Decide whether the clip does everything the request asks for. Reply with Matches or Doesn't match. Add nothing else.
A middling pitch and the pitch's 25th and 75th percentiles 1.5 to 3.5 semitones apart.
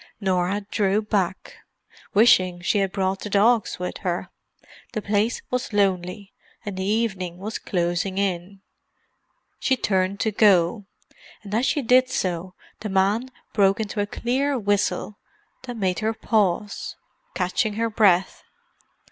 Doesn't match